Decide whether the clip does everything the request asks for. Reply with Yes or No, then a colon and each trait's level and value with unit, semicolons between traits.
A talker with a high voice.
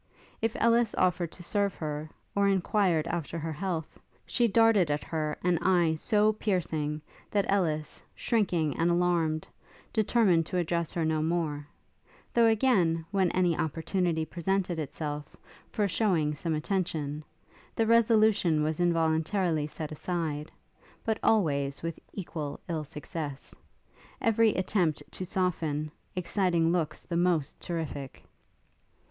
No: medium, 170 Hz